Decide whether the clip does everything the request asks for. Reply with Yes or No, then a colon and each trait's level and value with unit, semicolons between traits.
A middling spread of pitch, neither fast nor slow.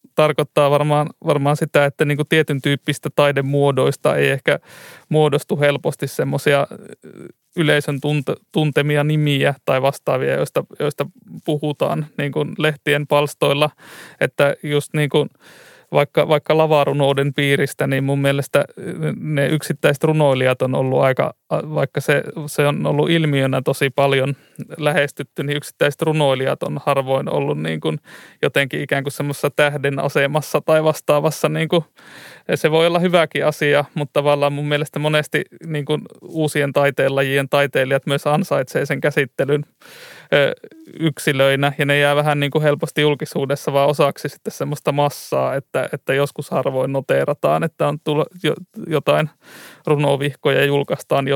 No: narrow, 1.4 semitones; average, 135 wpm